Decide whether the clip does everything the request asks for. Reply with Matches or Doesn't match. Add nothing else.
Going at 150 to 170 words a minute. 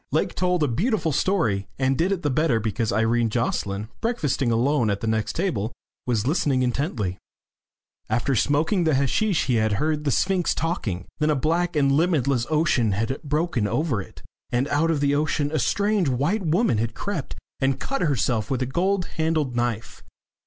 Doesn't match